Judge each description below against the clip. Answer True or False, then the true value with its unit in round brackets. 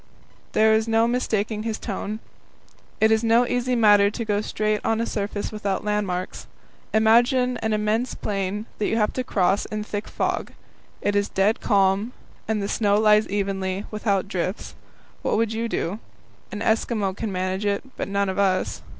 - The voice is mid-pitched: False (210 Hz)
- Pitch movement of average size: False (1.9 semitones)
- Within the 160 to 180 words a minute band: True (175 wpm)